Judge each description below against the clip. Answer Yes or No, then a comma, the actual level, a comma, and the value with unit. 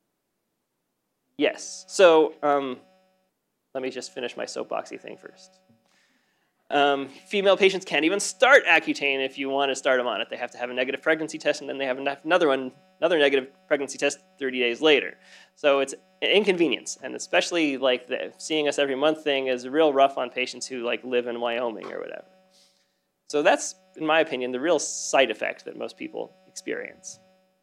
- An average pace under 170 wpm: No, average, 185 wpm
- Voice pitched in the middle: Yes, medium, 150 Hz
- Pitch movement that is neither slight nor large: No, wide, 5.9 semitones